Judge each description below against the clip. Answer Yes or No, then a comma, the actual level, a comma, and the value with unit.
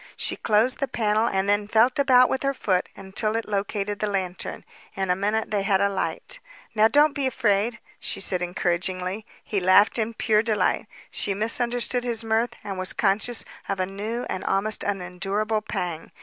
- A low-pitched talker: No, high, 210 Hz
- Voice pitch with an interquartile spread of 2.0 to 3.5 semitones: Yes, average, 2.9 semitones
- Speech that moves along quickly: No, average, 185 wpm